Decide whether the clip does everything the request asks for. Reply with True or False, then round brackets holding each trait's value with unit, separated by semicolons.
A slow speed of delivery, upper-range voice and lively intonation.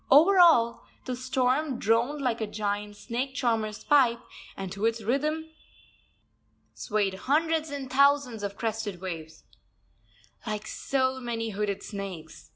False (130 wpm; 235 Hz; 4.9 semitones)